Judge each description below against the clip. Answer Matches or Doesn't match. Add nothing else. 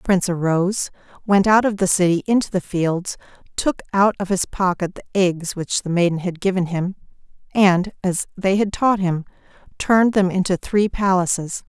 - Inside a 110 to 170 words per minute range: Doesn't match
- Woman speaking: Matches